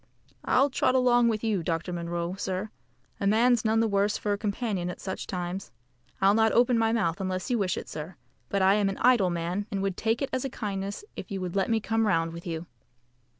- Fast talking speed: Yes, fast, 230 wpm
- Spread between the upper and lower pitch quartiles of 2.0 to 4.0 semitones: Yes, average, 3.5 semitones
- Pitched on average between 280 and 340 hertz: No, high, 200 Hz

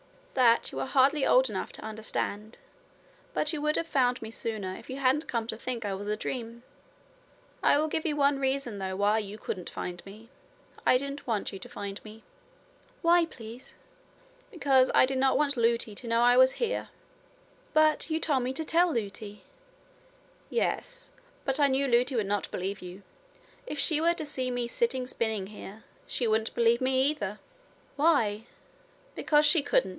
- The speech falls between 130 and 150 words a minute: No, average, 180 wpm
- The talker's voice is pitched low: No, very high, 250 Hz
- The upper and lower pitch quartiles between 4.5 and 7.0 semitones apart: Yes, average, 4.9 semitones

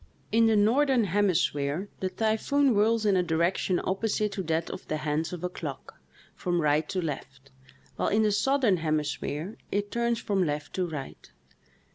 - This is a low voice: No, medium, 185 Hz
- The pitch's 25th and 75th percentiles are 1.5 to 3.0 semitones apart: No, wide, 5.4 semitones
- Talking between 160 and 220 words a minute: Yes, average, 170 wpm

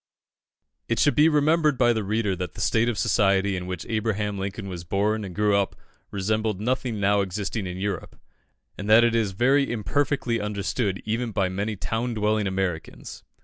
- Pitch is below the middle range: Yes, low, 105 Hz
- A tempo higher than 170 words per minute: Yes, average, 180 wpm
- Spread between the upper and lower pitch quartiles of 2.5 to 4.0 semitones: Yes, average, 3.0 semitones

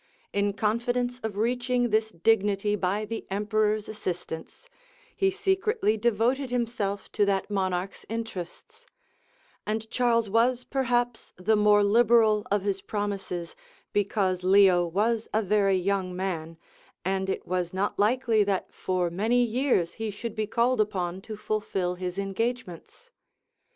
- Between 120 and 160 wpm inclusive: Yes, slow, 135 wpm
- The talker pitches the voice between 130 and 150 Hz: No, high, 210 Hz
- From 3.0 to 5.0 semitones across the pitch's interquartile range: Yes, average, 3.4 semitones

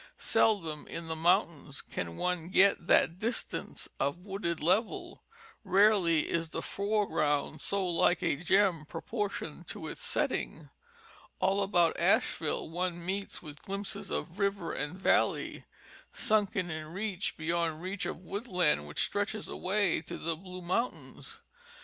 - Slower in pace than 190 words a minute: Yes, average, 140 wpm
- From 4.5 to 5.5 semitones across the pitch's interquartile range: No, average, 3.4 semitones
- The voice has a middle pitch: Yes, medium, 180 Hz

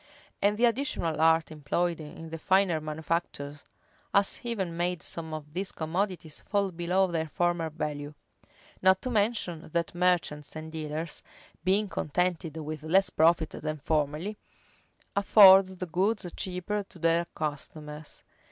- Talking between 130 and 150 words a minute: Yes, slow, 135 wpm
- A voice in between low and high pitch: Yes, medium, 170 Hz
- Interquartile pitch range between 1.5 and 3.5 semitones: Yes, average, 3.2 semitones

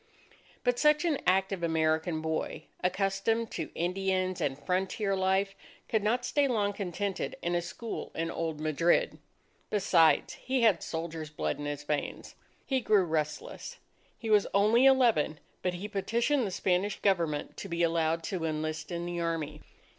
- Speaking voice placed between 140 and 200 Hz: Yes, medium, 185 Hz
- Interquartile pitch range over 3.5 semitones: Yes, average, 4.3 semitones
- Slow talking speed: No, average, 155 wpm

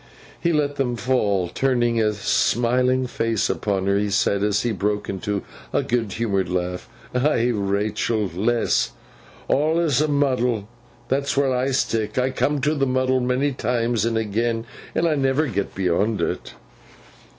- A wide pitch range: No, average, 4.2 semitones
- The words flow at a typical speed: Yes, average, 155 wpm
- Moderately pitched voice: No, low, 120 Hz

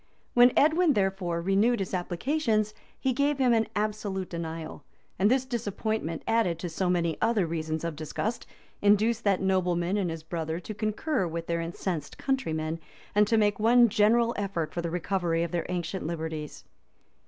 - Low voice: No, high, 195 Hz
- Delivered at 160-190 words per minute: Yes, average, 165 wpm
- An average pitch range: Yes, average, 4.9 semitones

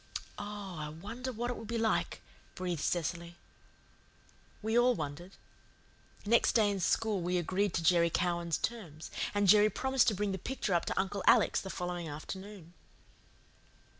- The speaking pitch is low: No, high, 190 Hz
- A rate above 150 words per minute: Yes, average, 160 wpm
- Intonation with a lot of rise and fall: No, average, 3.8 semitones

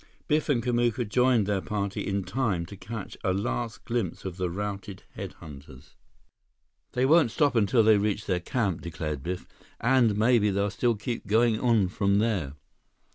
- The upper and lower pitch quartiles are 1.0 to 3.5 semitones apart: No, average, 3.9 semitones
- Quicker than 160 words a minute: Yes, average, 170 wpm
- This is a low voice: Yes, low, 105 Hz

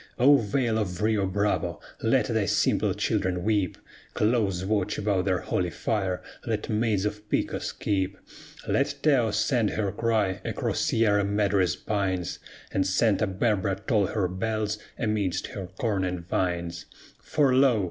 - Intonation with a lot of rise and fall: No, average, 2.9 semitones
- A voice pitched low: Yes, low, 105 Hz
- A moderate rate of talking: Yes, average, 145 wpm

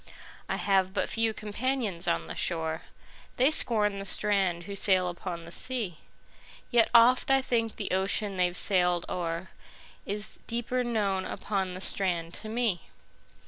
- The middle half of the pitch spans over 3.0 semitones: Yes, average, 4.2 semitones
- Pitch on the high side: Yes, high, 195 Hz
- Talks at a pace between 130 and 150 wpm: Yes, average, 140 wpm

